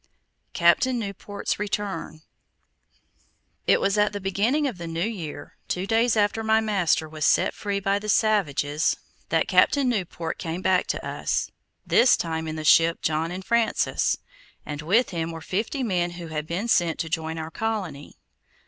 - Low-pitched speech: No, high, 190 Hz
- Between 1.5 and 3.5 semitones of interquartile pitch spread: No, average, 4.9 semitones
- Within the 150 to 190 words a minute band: Yes, average, 165 wpm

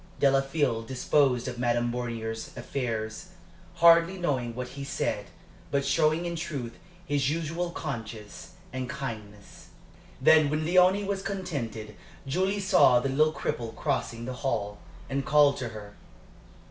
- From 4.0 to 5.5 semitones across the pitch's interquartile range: Yes, average, 5.1 semitones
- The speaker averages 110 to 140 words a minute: Yes, slow, 135 wpm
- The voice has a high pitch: No, low, 135 Hz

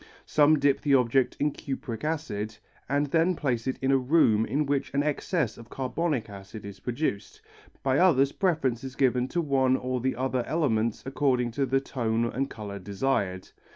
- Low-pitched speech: Yes, low, 130 Hz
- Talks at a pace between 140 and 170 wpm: No, average, 180 wpm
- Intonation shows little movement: No, average, 3.7 semitones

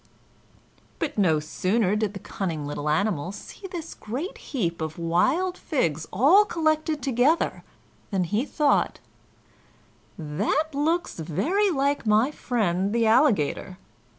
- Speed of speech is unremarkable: No, slow, 125 wpm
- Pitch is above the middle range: Yes, high, 220 Hz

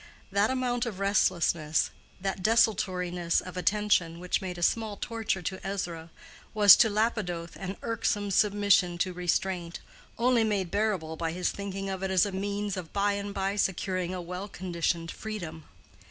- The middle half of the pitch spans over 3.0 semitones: No, average, 2.7 semitones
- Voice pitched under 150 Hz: No, high, 190 Hz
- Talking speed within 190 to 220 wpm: No, average, 160 wpm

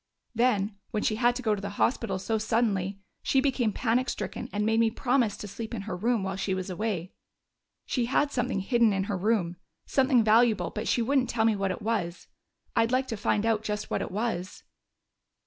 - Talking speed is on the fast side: Yes, fast, 210 wpm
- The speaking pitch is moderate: No, high, 220 Hz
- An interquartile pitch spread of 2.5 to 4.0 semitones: Yes, average, 3.3 semitones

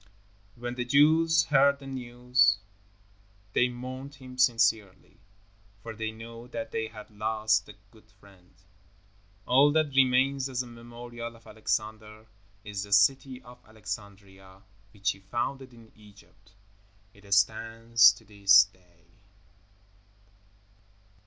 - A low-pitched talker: Yes, low, 115 Hz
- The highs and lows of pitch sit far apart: No, average, 3.5 semitones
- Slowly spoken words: Yes, slow, 120 wpm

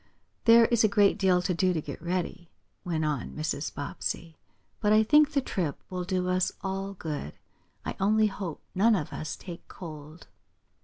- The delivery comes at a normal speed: Yes, average, 175 wpm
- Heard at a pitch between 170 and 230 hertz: Yes, medium, 185 Hz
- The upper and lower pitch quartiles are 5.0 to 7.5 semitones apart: No, average, 4.4 semitones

